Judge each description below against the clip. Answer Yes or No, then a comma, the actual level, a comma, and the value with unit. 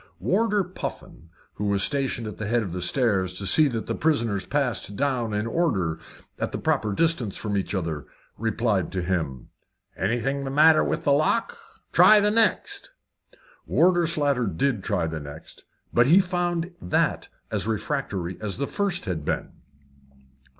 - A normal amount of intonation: No, wide, 8.4 semitones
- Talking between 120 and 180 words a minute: Yes, average, 165 wpm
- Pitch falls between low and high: No, low, 115 Hz